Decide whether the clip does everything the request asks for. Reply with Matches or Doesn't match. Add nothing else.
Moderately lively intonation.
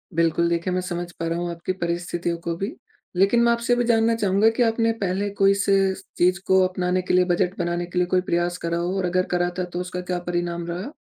Doesn't match